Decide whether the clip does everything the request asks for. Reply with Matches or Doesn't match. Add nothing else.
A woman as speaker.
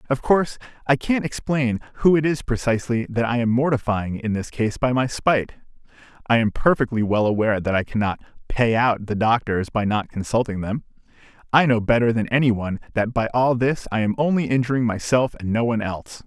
Doesn't match